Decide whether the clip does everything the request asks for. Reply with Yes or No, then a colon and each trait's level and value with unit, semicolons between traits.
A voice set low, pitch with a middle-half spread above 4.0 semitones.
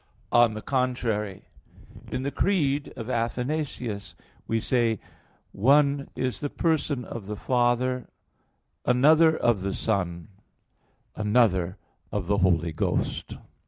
Yes: low, 120 Hz; average, 4.8 semitones